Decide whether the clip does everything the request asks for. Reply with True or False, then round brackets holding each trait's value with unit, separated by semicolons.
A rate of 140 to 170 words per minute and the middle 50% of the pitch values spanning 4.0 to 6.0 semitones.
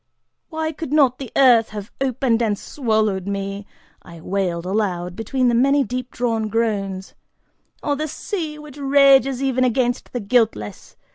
True (150 wpm; 5.2 semitones)